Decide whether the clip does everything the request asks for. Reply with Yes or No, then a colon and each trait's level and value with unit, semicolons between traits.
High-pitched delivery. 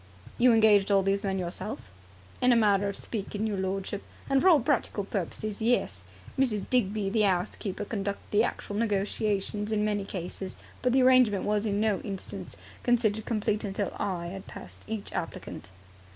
Yes: high, 205 Hz